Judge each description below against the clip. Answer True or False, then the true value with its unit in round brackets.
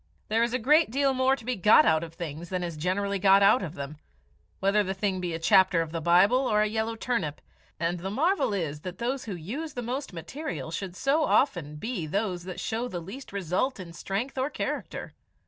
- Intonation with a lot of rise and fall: True (6.2 semitones)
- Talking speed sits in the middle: False (220 wpm)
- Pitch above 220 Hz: False (195 Hz)